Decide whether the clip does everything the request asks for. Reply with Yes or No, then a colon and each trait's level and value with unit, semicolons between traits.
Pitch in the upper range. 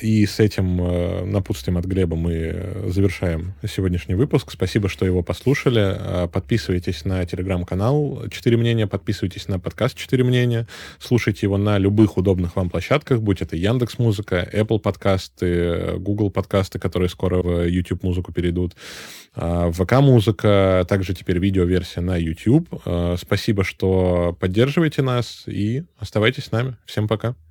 No: low, 100 Hz